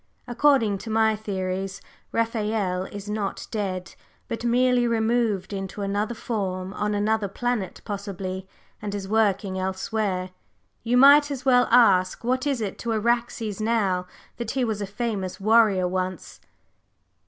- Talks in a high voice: Yes, high, 210 Hz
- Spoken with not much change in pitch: No, average, 3.3 semitones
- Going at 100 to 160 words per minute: Yes, average, 140 wpm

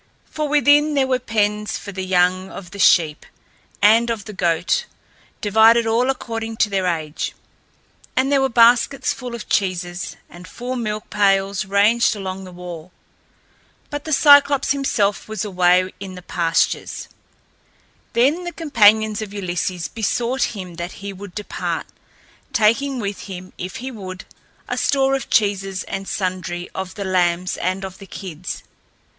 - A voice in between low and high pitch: No, high, 205 Hz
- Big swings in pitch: No, average, 4.3 semitones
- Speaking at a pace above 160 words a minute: No, average, 155 wpm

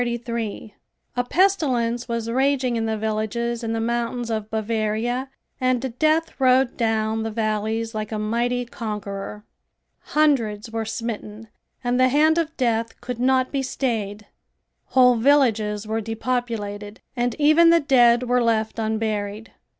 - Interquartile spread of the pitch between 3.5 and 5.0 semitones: No, narrow, 2.6 semitones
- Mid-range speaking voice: No, high, 230 Hz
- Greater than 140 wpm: No, slow, 135 wpm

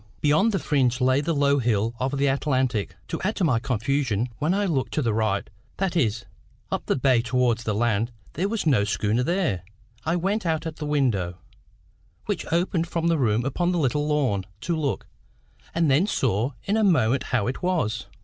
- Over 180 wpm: Yes, average, 195 wpm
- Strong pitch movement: Yes, wide, 6.0 semitones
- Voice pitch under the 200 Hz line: Yes, low, 135 Hz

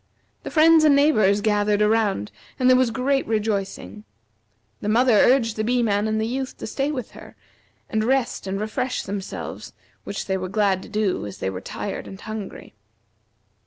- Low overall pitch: No, high, 215 Hz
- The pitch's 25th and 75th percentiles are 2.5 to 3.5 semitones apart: No, average, 4.1 semitones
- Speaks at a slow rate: No, average, 180 wpm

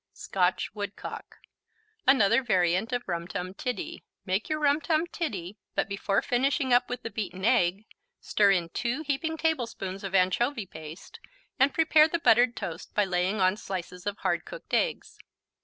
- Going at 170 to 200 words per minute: No, average, 160 wpm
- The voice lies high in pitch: Yes, high, 215 Hz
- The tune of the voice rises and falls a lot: Yes, wide, 6.4 semitones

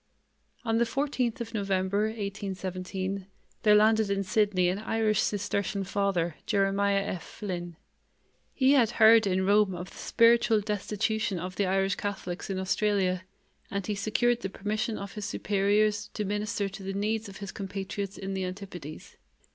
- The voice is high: Yes, high, 200 Hz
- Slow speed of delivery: No, average, 155 wpm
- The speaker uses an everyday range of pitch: No, narrow, 2.1 semitones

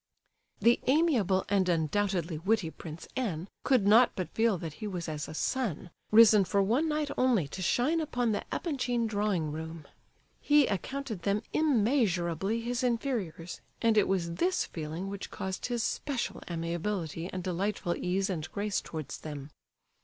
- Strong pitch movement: Yes, wide, 5.8 semitones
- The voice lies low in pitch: No, high, 200 Hz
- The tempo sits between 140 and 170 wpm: Yes, average, 155 wpm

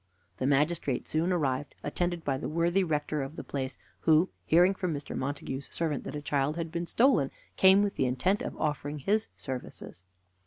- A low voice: No, medium, 155 Hz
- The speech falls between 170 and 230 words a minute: Yes, average, 185 wpm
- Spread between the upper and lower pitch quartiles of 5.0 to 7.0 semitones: No, average, 4.0 semitones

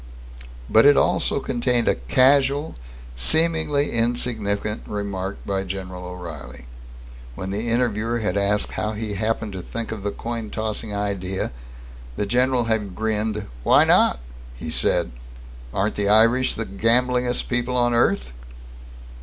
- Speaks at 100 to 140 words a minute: Yes, slow, 135 wpm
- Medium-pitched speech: No, low, 110 Hz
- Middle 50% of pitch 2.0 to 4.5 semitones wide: Yes, average, 3.4 semitones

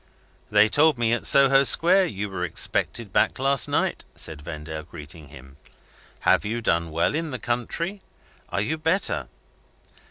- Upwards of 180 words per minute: No, average, 155 wpm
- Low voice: Yes, low, 115 Hz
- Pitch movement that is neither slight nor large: No, wide, 8.9 semitones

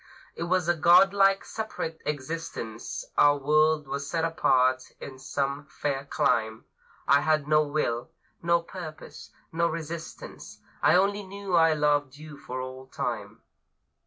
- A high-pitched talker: No, medium, 155 Hz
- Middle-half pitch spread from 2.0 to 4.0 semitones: Yes, average, 3.3 semitones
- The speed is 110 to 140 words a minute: Yes, slow, 135 wpm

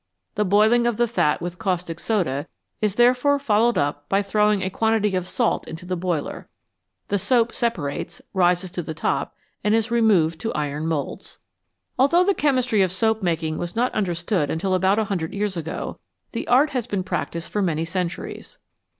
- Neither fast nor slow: Yes, average, 180 wpm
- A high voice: Yes, high, 195 Hz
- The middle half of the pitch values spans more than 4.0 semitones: Yes, average, 4.8 semitones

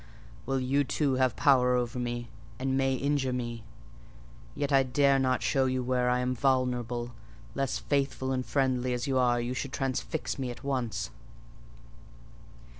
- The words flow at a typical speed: Yes, average, 160 wpm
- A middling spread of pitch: No, narrow, 1.4 semitones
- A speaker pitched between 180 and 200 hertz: No, low, 130 Hz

